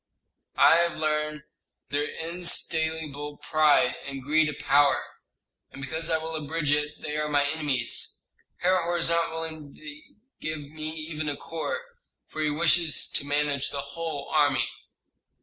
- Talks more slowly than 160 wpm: Yes, average, 150 wpm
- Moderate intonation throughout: No, narrow, 1.8 semitones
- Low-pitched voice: No, medium, 150 Hz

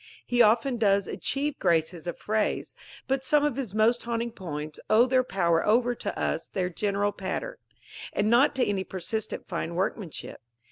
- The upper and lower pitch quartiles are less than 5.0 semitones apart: Yes, average, 4.5 semitones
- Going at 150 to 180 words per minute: Yes, average, 170 wpm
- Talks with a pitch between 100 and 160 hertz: No, high, 215 Hz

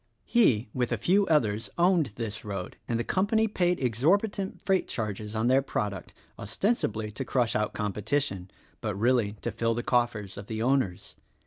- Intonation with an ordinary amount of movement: No, wide, 6.7 semitones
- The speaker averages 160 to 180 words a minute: Yes, average, 175 wpm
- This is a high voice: No, low, 115 Hz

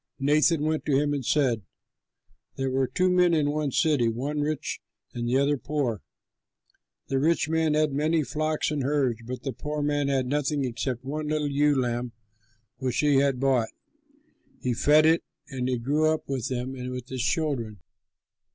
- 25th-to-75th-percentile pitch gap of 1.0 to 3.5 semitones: Yes, average, 2.9 semitones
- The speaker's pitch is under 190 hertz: Yes, medium, 140 Hz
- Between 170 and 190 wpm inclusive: Yes, average, 180 wpm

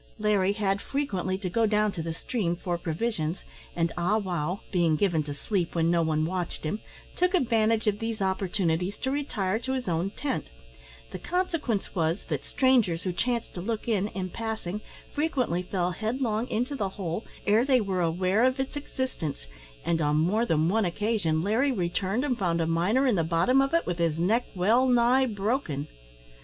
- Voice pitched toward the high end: Yes, high, 200 Hz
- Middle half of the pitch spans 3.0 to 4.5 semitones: No, wide, 5.4 semitones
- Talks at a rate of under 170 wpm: No, average, 185 wpm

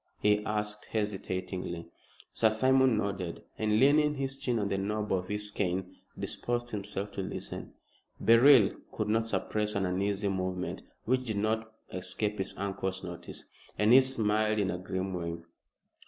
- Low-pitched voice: Yes, low, 105 Hz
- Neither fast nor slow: Yes, average, 155 wpm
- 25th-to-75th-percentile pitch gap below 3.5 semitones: Yes, average, 2.8 semitones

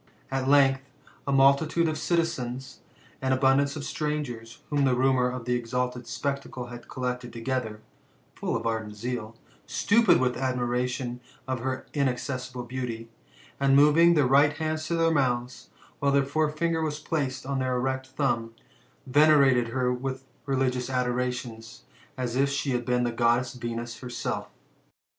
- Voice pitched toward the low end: Yes, low, 130 Hz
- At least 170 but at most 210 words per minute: No, average, 155 wpm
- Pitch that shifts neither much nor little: No, narrow, 2.3 semitones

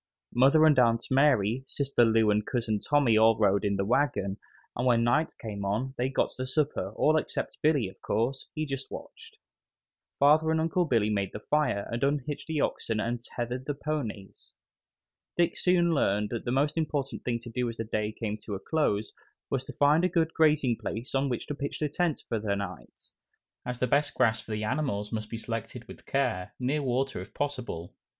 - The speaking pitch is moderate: No, low, 125 Hz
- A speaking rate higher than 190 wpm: Yes, average, 200 wpm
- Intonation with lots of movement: No, average, 5.0 semitones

